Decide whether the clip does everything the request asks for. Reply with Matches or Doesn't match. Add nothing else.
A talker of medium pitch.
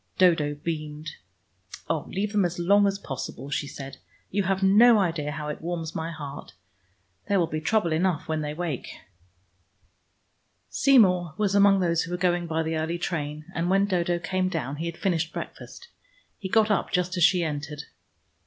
Matches